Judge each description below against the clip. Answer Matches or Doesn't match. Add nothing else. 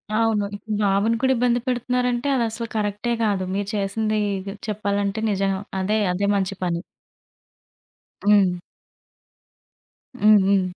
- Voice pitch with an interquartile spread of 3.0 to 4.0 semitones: Doesn't match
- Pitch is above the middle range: Matches